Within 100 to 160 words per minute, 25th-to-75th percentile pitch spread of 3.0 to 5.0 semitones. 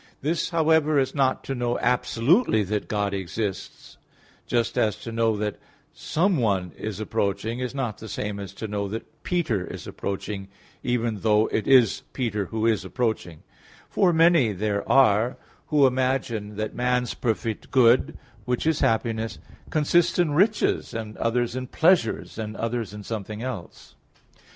Yes: average, 150 wpm; average, 4.0 semitones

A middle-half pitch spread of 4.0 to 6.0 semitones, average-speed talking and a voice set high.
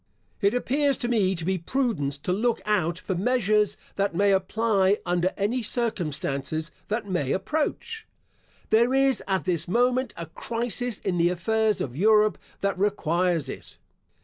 Yes: average, 4.9 semitones; average, 150 wpm; high, 200 Hz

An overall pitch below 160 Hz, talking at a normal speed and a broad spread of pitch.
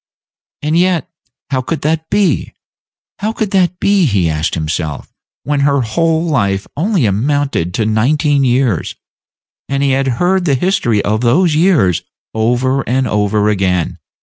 Yes: low, 135 Hz; average, 150 wpm; wide, 7.3 semitones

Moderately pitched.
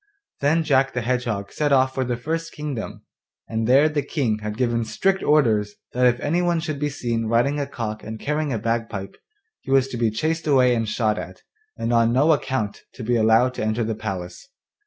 No: low, 125 Hz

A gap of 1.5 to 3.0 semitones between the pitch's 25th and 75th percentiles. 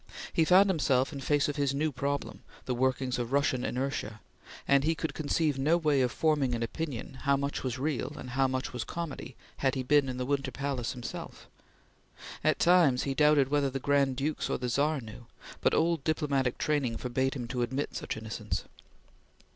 Yes: narrow, 2.6 semitones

